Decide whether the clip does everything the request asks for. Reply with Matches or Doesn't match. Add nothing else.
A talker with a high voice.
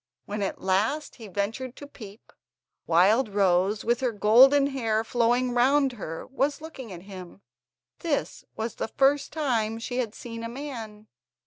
Matches